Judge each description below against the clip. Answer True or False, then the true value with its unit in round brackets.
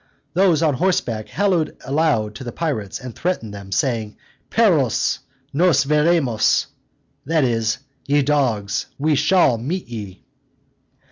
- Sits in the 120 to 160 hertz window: True (140 Hz)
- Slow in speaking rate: True (125 wpm)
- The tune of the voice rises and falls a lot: True (6.4 semitones)